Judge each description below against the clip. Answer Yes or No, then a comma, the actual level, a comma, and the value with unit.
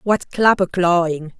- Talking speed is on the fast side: No, slow, 130 wpm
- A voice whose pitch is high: No, medium, 180 Hz